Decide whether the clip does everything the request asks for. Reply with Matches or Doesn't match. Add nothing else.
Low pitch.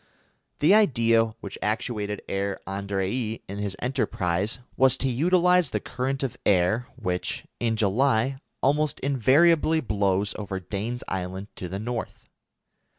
Matches